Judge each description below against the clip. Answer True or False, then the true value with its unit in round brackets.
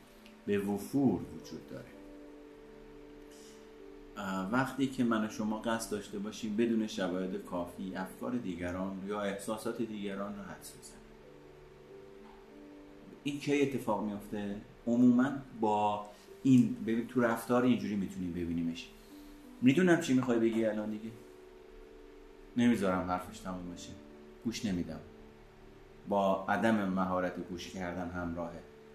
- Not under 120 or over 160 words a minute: False (110 wpm)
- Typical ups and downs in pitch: True (4.6 semitones)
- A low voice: True (100 Hz)